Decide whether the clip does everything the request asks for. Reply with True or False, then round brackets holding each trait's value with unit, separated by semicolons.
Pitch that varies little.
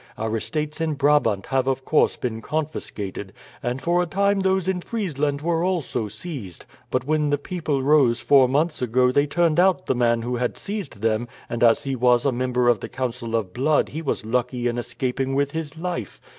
False (4.5 semitones)